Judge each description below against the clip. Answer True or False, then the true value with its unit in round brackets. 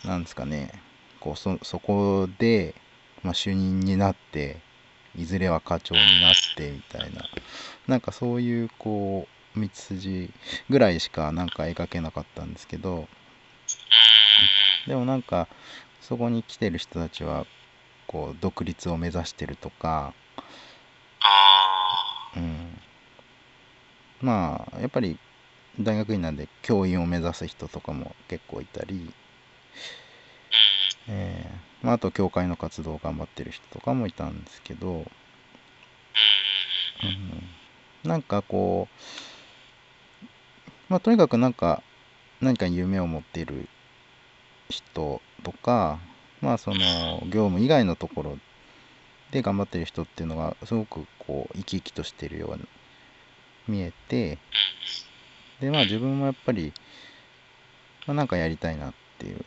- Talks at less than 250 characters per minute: True (240 characters per minute)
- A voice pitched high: False (95 Hz)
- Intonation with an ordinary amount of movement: True (4.8 semitones)